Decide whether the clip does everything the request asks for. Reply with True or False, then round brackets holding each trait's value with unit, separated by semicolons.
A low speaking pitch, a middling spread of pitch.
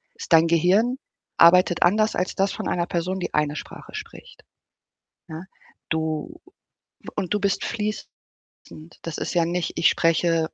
False (175 Hz; 3.4 semitones)